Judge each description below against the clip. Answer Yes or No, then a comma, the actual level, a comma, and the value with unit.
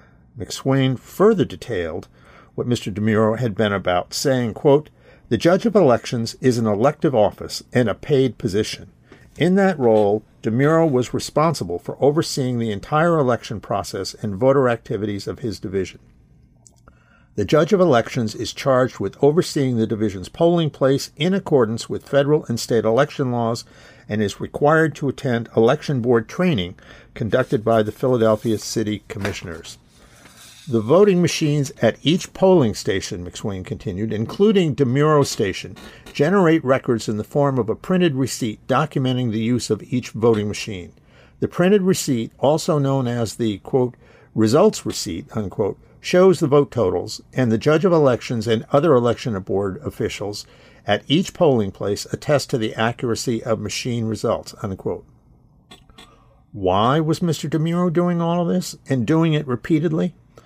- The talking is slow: No, average, 150 wpm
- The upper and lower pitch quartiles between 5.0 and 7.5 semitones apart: Yes, wide, 5.4 semitones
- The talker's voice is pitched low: Yes, low, 130 Hz